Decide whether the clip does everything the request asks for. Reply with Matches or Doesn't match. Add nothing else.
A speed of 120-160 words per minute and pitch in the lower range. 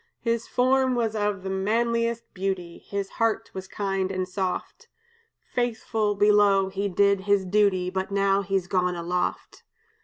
Doesn't match